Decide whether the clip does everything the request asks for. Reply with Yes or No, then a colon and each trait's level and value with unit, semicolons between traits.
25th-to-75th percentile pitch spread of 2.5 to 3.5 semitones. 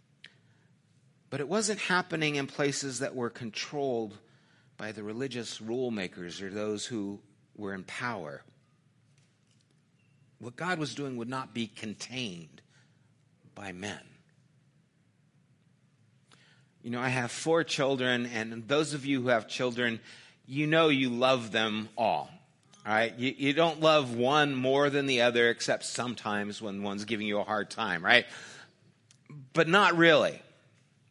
No: average, 4.2 semitones